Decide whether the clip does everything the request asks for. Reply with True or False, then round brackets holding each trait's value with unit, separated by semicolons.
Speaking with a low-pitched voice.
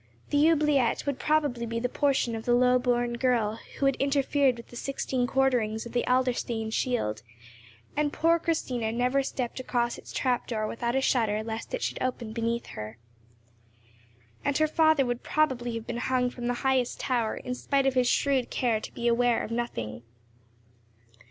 False (245 Hz)